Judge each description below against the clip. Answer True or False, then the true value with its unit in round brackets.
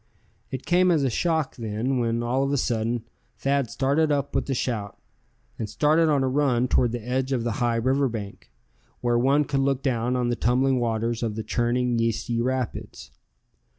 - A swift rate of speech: False (190 wpm)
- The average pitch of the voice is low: True (125 Hz)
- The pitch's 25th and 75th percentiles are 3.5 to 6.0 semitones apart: False (2.8 semitones)